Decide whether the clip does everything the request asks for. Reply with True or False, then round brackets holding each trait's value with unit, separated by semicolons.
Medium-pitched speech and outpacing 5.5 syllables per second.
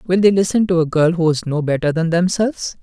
True (175 Hz; 6.0 syllables/s)